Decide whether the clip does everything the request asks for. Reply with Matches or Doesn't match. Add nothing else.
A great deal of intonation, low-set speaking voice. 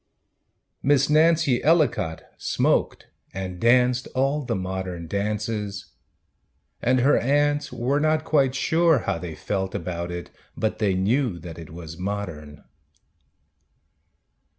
Matches